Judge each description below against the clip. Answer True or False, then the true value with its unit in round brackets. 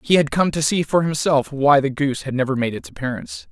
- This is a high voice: False (145 Hz)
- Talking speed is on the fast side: True (255 wpm)